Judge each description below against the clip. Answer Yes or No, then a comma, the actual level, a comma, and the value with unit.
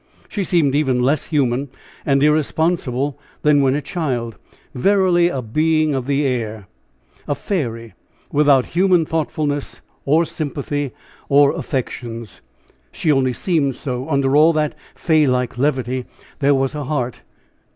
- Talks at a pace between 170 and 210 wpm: No, slow, 135 wpm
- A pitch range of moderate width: Yes, average, 3.3 semitones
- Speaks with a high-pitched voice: No, medium, 140 Hz